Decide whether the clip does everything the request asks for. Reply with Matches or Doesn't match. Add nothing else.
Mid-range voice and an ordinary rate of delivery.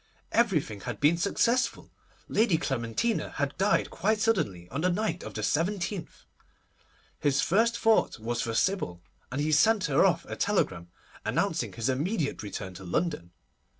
Matches